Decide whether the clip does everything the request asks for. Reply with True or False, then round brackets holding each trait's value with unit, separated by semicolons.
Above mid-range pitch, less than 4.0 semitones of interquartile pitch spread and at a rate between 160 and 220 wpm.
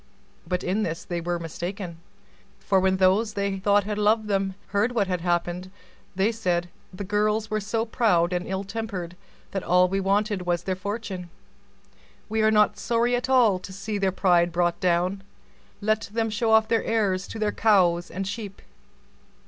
True (195 Hz; 3.0 semitones; 165 wpm)